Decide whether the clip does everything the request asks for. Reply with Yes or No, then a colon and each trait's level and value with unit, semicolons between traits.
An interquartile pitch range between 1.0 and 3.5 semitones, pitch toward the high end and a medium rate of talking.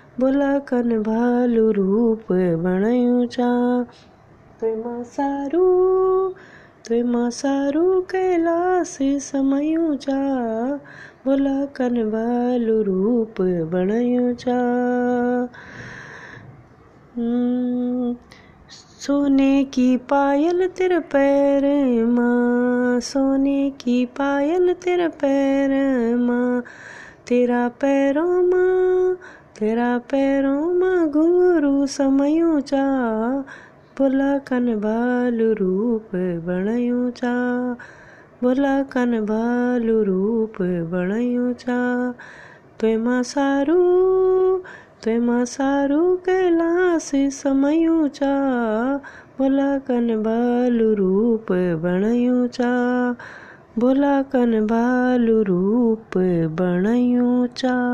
No: average, 2.9 semitones; high, 245 Hz; slow, 60 wpm